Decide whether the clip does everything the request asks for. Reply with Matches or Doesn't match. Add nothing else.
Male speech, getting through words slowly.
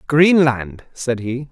Matches